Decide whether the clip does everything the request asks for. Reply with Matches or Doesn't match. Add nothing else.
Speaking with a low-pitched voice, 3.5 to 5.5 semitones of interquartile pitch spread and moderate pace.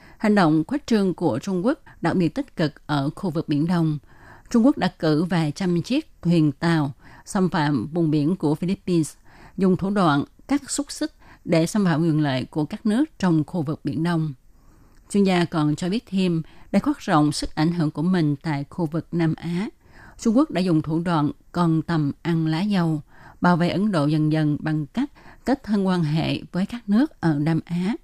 Doesn't match